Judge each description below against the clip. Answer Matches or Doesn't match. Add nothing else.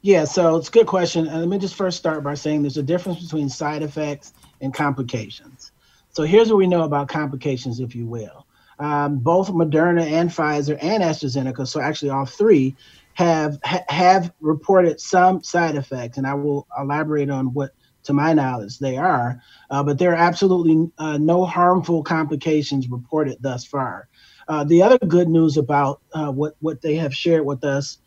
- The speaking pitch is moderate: Matches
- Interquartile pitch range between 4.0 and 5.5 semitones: Doesn't match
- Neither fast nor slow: Matches